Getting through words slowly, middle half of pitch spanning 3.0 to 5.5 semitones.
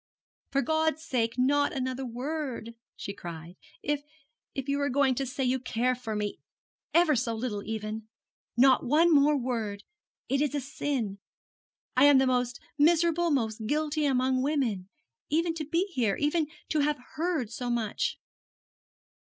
No: average, 155 wpm; average, 4.2 semitones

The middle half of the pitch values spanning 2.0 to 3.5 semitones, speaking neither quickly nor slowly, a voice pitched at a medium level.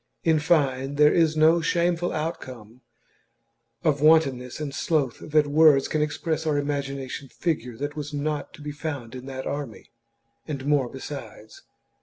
Yes: narrow, 2.6 semitones; average, 150 wpm; medium, 145 Hz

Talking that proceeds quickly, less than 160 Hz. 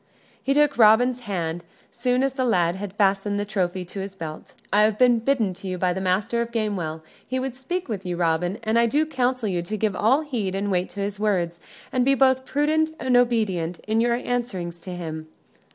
No: fast, 215 wpm; high, 210 Hz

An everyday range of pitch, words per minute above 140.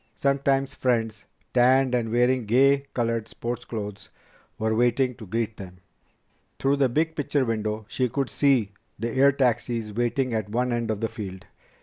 Yes: average, 3.1 semitones; average, 160 wpm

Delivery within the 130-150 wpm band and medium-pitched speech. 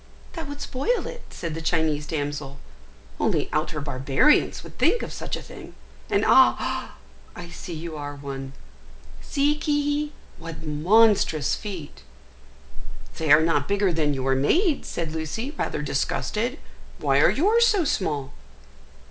Yes: average, 145 wpm; medium, 165 Hz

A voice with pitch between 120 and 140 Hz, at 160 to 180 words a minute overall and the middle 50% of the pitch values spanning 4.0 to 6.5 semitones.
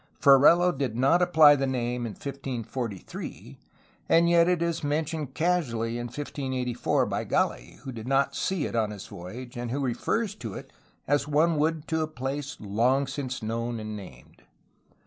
Yes: low, 135 Hz; average, 165 wpm; average, 4.6 semitones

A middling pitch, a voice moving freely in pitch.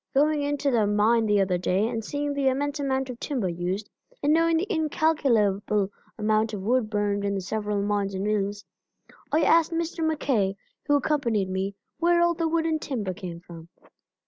No: high, 225 Hz; wide, 6.5 semitones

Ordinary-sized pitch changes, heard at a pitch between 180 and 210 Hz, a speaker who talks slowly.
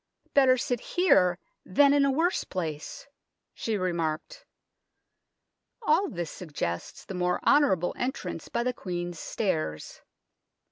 No: wide, 8.0 semitones; medium, 185 Hz; slow, 125 wpm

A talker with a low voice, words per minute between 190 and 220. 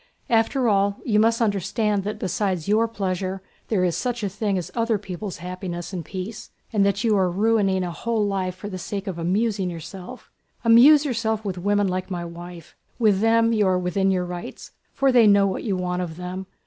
No: high, 195 Hz; average, 200 wpm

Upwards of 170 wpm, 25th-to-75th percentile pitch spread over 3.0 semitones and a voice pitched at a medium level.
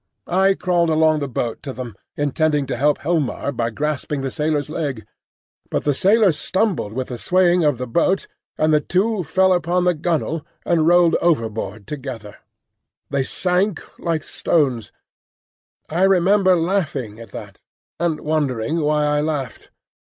No: average, 150 wpm; average, 4.6 semitones; medium, 155 Hz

